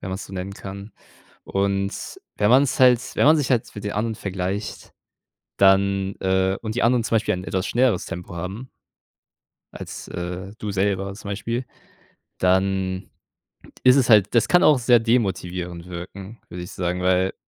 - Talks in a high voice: No, low, 100 Hz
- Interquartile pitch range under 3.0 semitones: No, average, 3.5 semitones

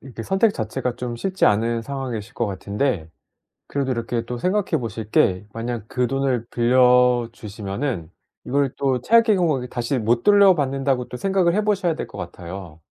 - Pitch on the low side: Yes, low, 125 Hz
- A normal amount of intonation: Yes, average, 3.8 semitones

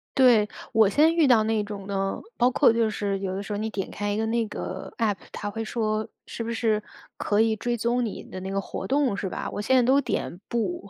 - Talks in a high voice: Yes, high, 220 Hz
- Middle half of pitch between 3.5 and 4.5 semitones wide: No, narrow, 2.6 semitones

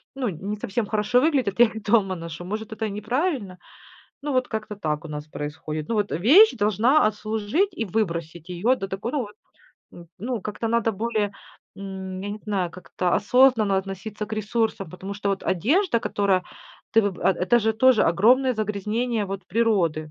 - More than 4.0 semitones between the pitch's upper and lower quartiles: No, average, 3.5 semitones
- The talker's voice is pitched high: Yes, high, 210 Hz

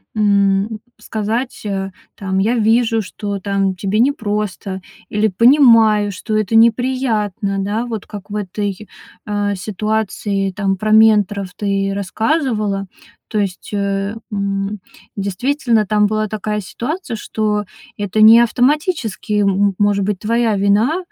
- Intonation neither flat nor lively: No, narrow, 2.0 semitones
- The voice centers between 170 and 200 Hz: No, high, 210 Hz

